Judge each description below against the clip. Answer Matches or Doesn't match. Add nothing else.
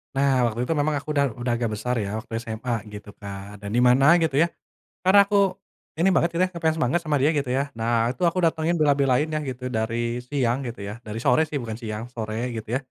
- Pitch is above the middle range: Doesn't match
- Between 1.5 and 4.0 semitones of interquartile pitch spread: Doesn't match